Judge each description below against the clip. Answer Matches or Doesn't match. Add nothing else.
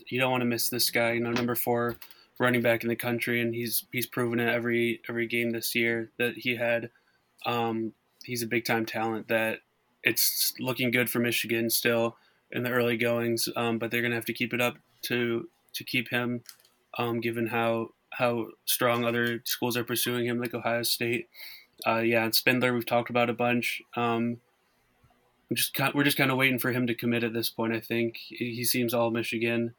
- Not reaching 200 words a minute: Doesn't match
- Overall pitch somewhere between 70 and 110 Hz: Doesn't match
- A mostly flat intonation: Matches